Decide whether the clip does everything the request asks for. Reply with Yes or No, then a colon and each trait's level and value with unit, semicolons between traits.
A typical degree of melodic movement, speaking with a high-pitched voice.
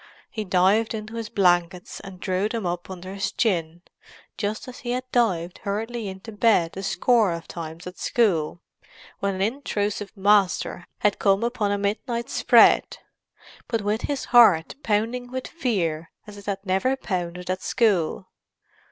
Yes: average, 3.8 semitones; high, 200 Hz